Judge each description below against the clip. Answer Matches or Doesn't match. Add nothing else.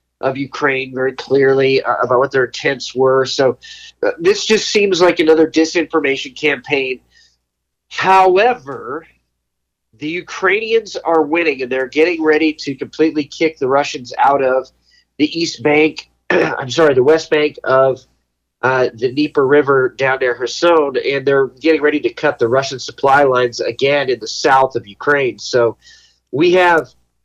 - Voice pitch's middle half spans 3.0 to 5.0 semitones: Matches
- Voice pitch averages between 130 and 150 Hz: Matches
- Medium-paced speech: Matches